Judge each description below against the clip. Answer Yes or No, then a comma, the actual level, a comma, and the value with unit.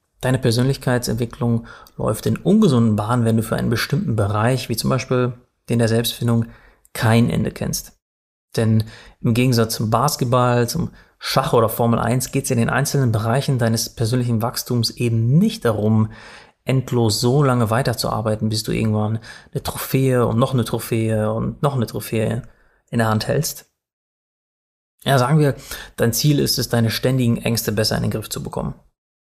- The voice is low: Yes, low, 120 Hz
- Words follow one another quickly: No, average, 165 wpm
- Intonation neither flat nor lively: No, narrow, 2.2 semitones